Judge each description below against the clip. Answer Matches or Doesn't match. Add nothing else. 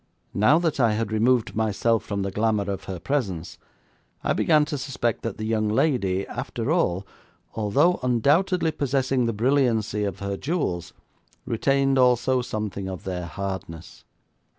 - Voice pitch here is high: Doesn't match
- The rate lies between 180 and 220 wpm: Doesn't match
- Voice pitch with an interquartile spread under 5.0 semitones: Doesn't match